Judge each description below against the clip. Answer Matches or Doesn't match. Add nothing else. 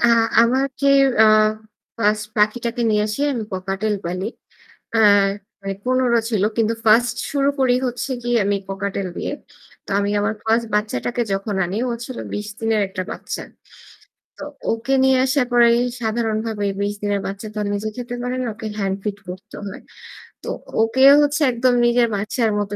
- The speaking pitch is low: Doesn't match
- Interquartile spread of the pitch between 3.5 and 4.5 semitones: Doesn't match